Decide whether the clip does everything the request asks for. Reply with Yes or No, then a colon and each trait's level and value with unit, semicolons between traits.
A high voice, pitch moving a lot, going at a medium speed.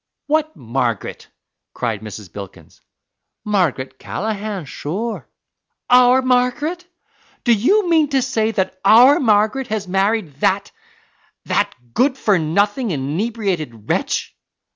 No: high, 210 Hz; wide, 8.3 semitones; slow, 110 wpm